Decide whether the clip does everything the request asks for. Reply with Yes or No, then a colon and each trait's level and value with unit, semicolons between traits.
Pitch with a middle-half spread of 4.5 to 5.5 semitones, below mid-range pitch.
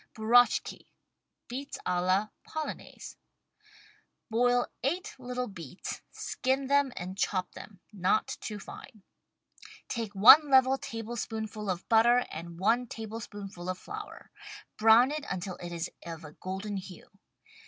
No: average, 4.9 semitones; high, 220 Hz